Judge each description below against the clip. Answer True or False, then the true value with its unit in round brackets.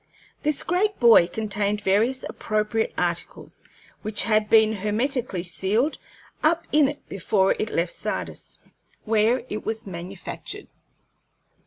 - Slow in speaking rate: True (120 wpm)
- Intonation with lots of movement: False (3.8 semitones)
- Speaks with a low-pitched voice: False (215 Hz)